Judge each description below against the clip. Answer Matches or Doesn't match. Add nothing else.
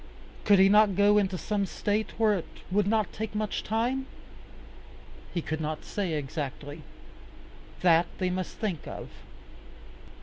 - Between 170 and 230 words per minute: Doesn't match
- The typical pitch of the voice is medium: Doesn't match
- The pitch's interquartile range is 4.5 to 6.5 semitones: Doesn't match